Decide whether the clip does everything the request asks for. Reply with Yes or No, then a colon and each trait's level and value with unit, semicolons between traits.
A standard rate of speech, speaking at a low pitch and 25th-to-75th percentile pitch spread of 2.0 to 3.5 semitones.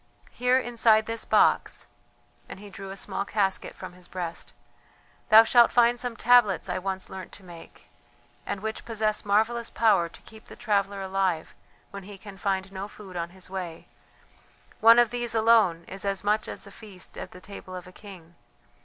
No: average, 185 wpm; high, 200 Hz; average, 2.8 semitones